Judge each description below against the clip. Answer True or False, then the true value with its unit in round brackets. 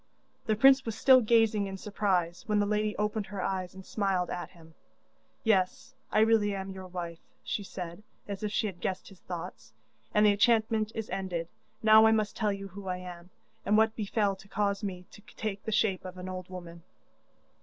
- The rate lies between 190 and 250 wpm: True (200 wpm)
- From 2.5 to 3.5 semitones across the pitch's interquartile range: True (2.8 semitones)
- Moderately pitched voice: False (200 Hz)